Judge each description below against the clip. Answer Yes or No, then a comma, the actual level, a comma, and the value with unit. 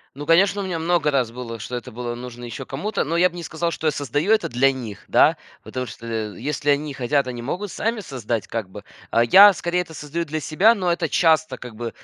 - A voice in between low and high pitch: Yes, medium, 145 Hz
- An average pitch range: No, wide, 5.9 semitones